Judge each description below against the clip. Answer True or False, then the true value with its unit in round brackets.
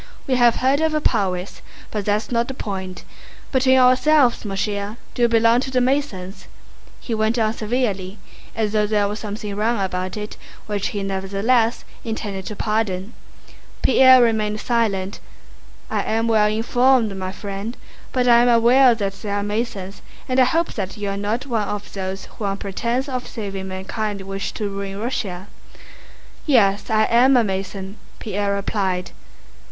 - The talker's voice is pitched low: False (215 Hz)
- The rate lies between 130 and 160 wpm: False (170 wpm)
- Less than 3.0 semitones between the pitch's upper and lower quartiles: False (3.3 semitones)